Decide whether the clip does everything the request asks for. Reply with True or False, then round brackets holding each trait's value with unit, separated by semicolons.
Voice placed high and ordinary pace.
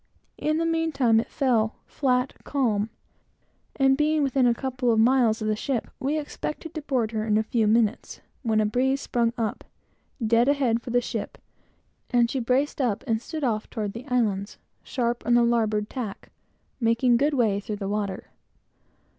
True (240 Hz; 180 wpm)